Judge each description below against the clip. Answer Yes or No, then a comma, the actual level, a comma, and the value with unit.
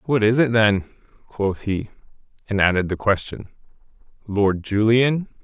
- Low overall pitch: Yes, low, 110 Hz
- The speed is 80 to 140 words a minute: Yes, slow, 135 wpm